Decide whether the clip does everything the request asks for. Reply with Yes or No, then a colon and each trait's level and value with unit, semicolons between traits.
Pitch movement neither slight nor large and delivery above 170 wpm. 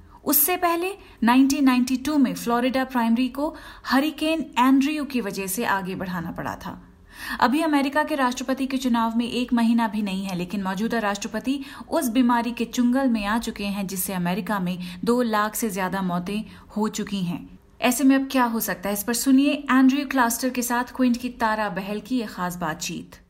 Yes: average, 4.2 semitones; average, 185 wpm